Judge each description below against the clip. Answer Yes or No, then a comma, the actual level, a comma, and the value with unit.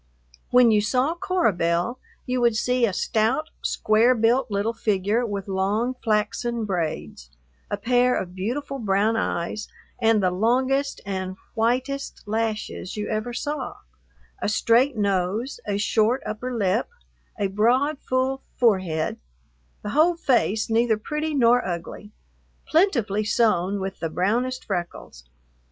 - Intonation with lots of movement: No, average, 4.0 semitones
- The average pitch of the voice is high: Yes, high, 225 Hz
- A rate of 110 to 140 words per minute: Yes, slow, 135 wpm